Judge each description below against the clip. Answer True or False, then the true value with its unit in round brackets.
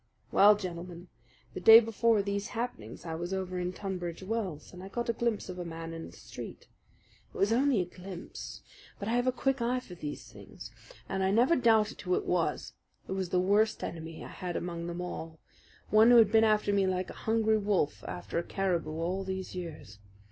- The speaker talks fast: True (210 wpm)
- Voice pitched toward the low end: False (190 Hz)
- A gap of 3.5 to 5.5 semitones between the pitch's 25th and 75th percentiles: True (4.1 semitones)